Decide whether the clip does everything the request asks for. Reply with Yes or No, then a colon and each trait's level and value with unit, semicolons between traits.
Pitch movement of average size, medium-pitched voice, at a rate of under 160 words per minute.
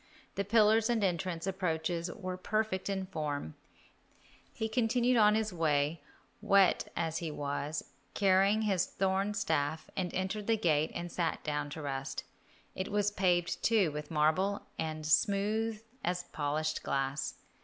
Yes: average, 4.7 semitones; medium, 180 Hz; average, 140 wpm